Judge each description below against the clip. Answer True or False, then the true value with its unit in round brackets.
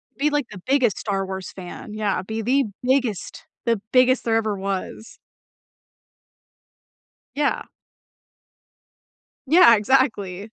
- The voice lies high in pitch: True (220 Hz)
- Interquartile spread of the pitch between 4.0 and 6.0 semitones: True (4.8 semitones)